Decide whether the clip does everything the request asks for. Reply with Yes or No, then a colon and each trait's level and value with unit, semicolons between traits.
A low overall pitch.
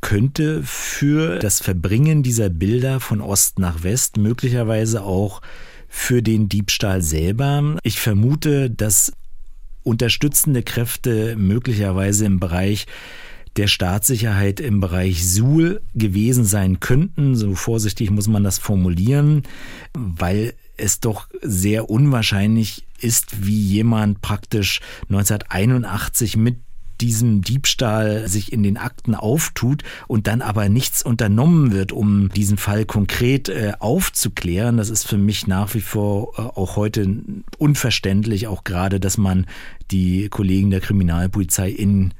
Yes: low, 105 Hz